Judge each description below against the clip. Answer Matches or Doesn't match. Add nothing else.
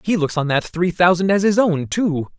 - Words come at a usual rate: Doesn't match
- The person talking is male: Matches